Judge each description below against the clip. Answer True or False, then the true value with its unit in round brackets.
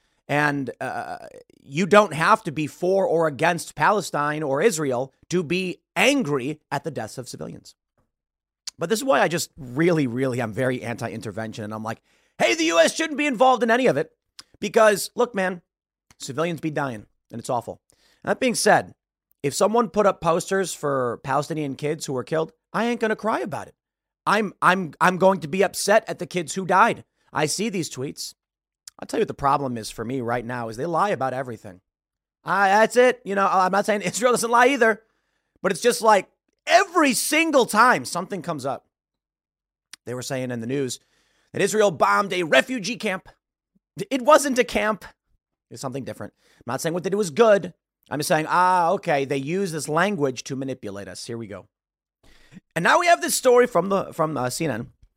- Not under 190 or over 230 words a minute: True (195 wpm)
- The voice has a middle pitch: True (170 Hz)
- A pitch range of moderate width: False (8.0 semitones)